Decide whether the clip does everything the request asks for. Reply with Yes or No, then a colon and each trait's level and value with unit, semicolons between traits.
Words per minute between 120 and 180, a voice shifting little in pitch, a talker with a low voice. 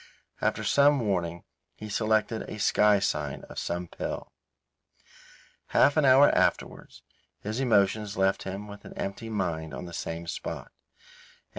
No: average, 140 wpm; average, 3.9 semitones; low, 100 Hz